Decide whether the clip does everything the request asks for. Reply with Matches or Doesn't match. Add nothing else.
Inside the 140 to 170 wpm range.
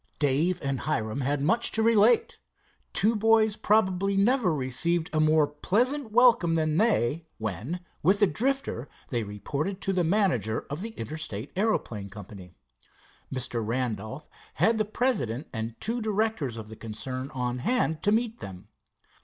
Matches